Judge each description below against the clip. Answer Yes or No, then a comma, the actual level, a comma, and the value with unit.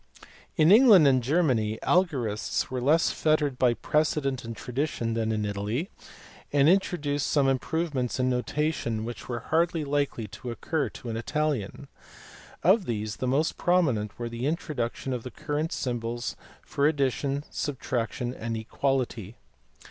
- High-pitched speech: No, low, 130 Hz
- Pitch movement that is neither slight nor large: Yes, average, 4.6 semitones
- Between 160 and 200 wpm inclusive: No, average, 145 wpm